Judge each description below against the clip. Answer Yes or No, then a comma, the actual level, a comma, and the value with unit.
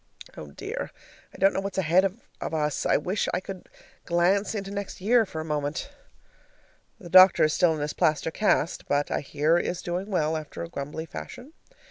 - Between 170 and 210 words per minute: Yes, average, 190 wpm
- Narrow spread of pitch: No, average, 4.0 semitones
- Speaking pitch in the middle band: Yes, medium, 175 Hz